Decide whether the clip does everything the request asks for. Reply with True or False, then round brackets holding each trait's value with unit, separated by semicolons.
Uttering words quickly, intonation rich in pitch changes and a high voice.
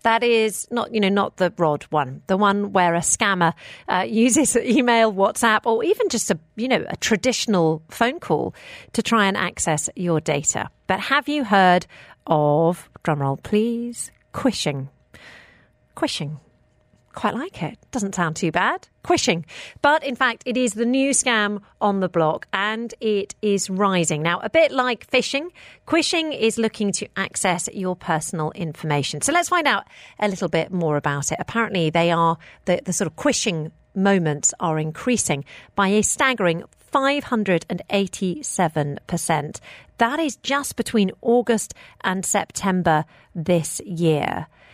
False (150 wpm; 6.1 semitones; 200 Hz)